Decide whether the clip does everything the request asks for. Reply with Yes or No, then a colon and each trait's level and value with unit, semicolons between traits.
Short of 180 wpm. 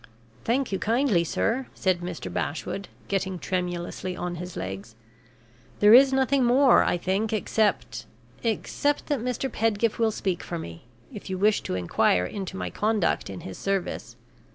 Yes: average, 155 wpm